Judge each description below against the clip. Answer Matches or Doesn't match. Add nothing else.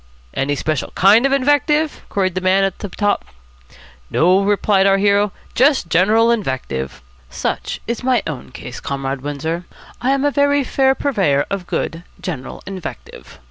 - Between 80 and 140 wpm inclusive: Doesn't match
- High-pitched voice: Matches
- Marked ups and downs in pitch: Matches